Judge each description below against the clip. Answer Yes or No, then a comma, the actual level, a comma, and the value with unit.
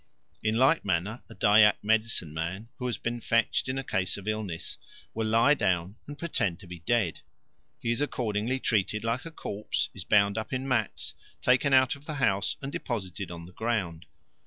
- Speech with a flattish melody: No, average, 4.7 semitones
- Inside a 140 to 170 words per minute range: No, average, 190 wpm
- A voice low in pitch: Yes, low, 110 Hz